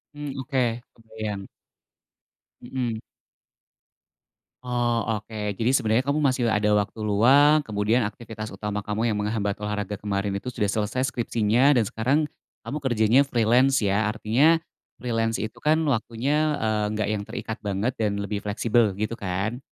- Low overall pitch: Yes, low, 110 Hz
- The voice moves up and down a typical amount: Yes, average, 3.1 semitones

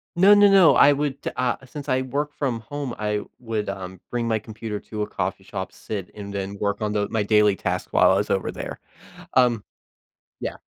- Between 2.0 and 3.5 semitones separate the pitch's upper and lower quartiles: No, average, 4.6 semitones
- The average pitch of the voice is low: Yes, low, 110 Hz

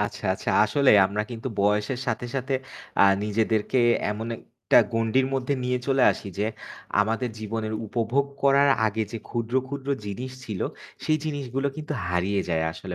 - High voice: No, low, 115 Hz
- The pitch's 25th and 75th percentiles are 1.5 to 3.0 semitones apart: No, average, 4.0 semitones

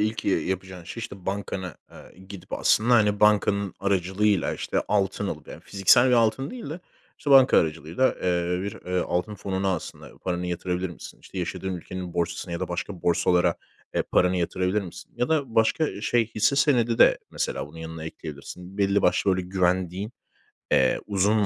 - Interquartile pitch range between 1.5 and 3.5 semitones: Yes, average, 3.1 semitones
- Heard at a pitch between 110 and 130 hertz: No, very low, 95 Hz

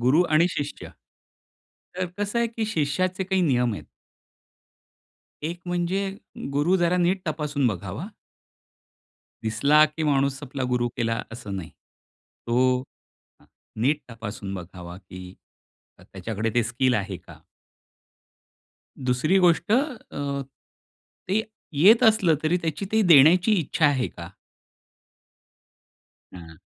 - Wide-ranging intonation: Yes, wide, 7.1 semitones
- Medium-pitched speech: Yes, medium, 145 Hz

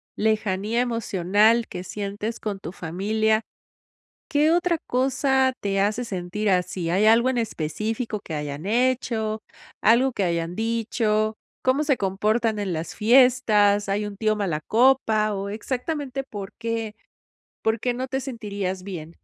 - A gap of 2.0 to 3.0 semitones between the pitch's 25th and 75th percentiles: No, average, 3.6 semitones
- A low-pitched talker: No, high, 215 Hz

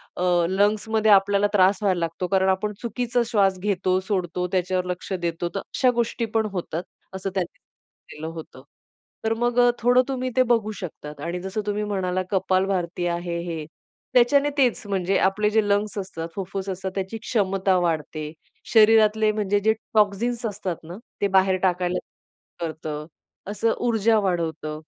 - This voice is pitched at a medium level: No, high, 195 Hz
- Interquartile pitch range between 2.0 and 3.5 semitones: Yes, average, 3.0 semitones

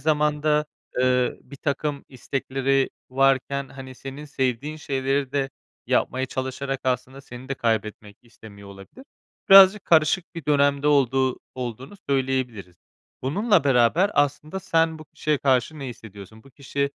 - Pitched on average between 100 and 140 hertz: Yes, low, 135 Hz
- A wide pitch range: No, average, 2.7 semitones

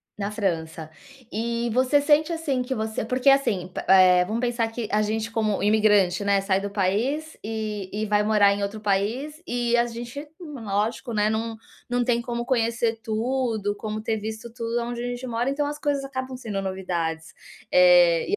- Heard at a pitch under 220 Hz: No, high, 225 Hz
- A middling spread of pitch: Yes, average, 3.3 semitones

